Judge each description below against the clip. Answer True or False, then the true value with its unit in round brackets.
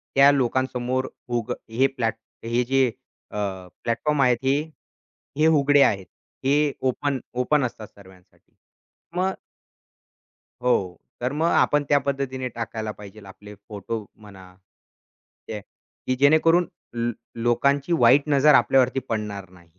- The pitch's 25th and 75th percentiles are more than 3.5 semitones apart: True (4.6 semitones)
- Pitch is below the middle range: True (125 Hz)